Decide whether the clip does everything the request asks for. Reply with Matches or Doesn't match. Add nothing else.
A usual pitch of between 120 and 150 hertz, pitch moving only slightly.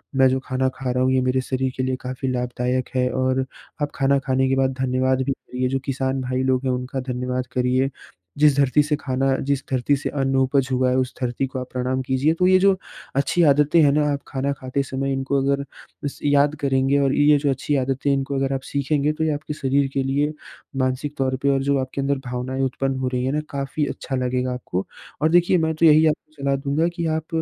Matches